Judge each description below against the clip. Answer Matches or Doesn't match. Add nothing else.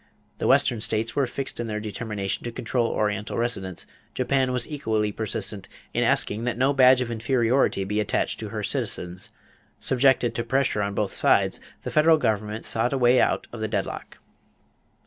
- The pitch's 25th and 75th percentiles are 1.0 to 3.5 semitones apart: Matches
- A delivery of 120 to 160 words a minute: Doesn't match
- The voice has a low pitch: Matches